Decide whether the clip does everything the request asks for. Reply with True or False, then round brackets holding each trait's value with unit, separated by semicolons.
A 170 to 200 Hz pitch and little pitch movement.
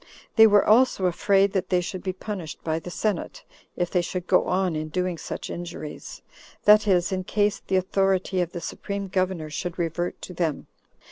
True (185 Hz; 2.1 semitones)